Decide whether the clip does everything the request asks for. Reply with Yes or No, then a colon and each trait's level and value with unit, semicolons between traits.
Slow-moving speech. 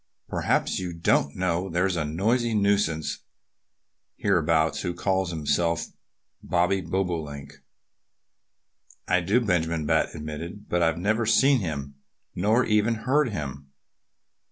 Yes: slow, 115 wpm